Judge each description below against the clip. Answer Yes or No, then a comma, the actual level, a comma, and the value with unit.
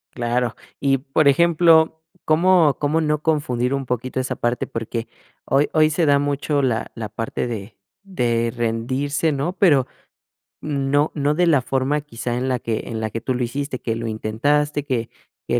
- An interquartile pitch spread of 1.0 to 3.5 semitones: No, average, 4.0 semitones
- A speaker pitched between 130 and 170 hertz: Yes, low, 135 Hz